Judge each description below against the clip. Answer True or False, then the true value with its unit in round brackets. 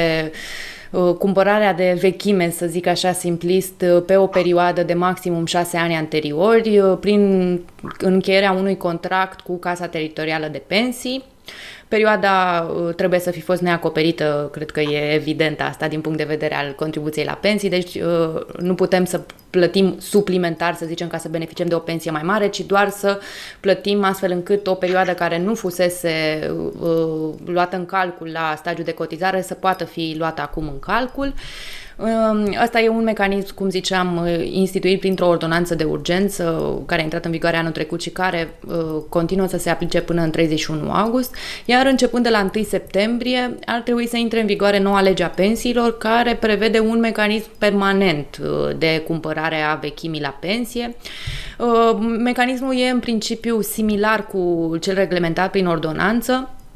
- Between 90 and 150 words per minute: False (165 wpm)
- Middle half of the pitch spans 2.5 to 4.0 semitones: True (3.5 semitones)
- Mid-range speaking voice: True (180 Hz)